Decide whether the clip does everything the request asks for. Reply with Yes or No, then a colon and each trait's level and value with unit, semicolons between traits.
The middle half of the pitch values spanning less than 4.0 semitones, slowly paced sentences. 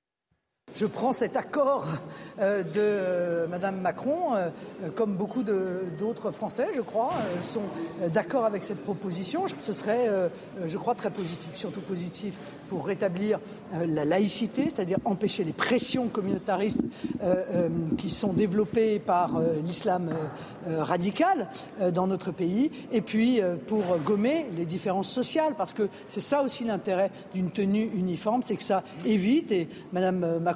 Yes: average, 3.5 semitones; slow, 135 wpm